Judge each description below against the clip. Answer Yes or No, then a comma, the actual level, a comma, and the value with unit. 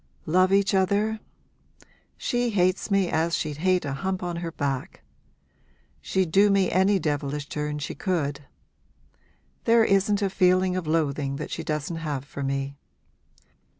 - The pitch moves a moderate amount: Yes, average, 4.6 semitones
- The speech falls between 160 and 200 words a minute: No, average, 150 wpm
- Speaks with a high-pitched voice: No, medium, 175 Hz